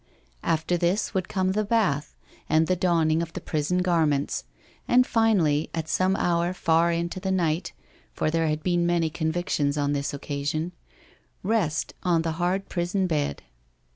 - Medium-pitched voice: Yes, medium, 170 Hz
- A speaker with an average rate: Yes, average, 155 wpm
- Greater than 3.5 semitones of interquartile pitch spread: No, average, 2.9 semitones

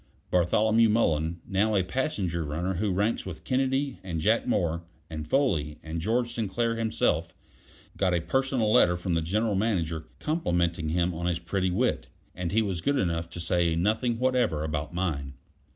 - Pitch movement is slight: No, average, 5.3 semitones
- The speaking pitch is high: No, very low, 90 Hz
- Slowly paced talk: No, average, 170 wpm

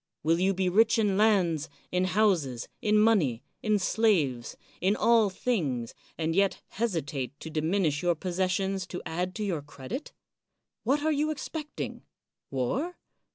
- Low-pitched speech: No, medium, 185 Hz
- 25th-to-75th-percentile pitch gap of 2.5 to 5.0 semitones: No, wide, 5.4 semitones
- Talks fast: No, average, 145 wpm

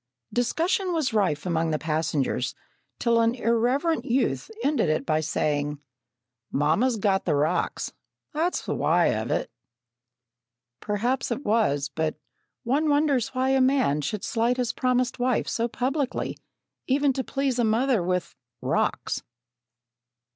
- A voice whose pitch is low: No, high, 235 Hz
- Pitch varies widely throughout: Yes, wide, 8.2 semitones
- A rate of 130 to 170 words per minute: Yes, slow, 135 wpm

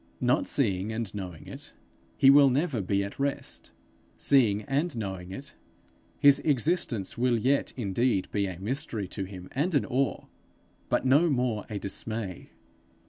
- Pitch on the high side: No, low, 115 Hz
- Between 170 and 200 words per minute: No, average, 150 wpm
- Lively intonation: Yes, wide, 5.7 semitones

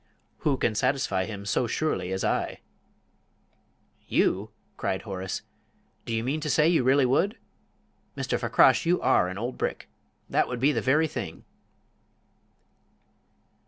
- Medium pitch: No, low, 125 Hz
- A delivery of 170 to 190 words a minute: No, average, 140 wpm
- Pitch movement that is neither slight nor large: No, wide, 7.0 semitones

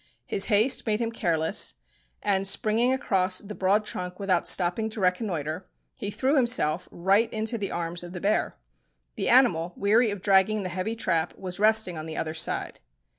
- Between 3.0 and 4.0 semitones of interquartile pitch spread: Yes, average, 3.6 semitones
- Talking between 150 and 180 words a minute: Yes, average, 175 wpm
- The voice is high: Yes, high, 195 Hz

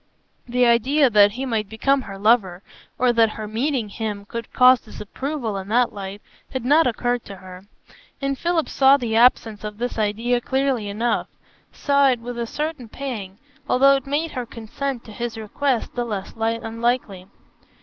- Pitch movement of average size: Yes, average, 3.7 semitones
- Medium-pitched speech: No, high, 235 Hz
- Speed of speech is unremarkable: Yes, average, 170 wpm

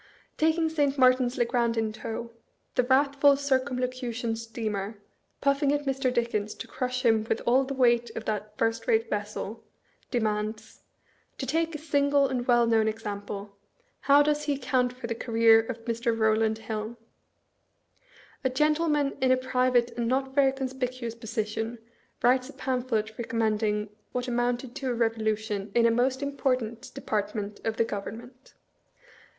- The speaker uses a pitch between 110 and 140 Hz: No, high, 240 Hz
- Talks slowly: No, average, 155 wpm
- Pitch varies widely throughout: No, average, 2.9 semitones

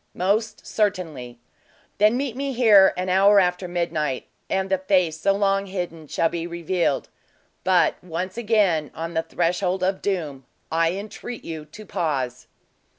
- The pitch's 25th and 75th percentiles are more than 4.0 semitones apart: No, average, 3.4 semitones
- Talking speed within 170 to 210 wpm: No, average, 150 wpm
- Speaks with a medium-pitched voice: Yes, medium, 180 Hz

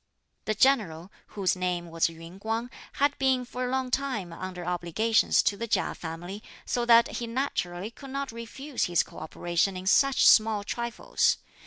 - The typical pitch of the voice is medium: No, high, 215 Hz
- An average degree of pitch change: No, wide, 5.9 semitones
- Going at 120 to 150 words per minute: No, average, 170 wpm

